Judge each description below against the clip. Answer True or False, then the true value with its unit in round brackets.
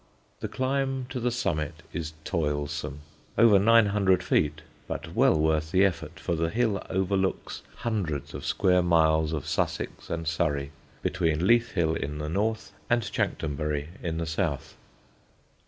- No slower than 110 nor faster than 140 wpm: False (150 wpm)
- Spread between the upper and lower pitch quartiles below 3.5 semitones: False (4.8 semitones)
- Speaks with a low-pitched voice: True (85 Hz)